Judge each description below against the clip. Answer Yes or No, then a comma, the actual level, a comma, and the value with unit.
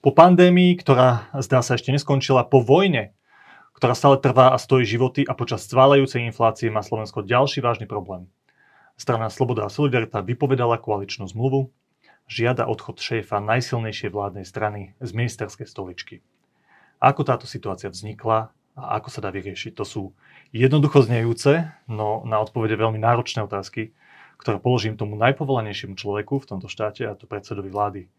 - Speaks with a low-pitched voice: Yes, low, 115 Hz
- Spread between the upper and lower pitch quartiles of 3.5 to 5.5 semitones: Yes, average, 3.9 semitones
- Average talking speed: Yes, average, 150 wpm